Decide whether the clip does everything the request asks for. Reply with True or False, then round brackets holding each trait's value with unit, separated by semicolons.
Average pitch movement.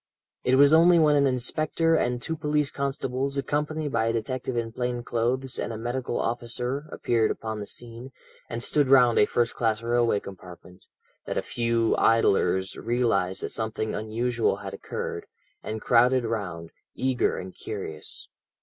True (3.1 semitones)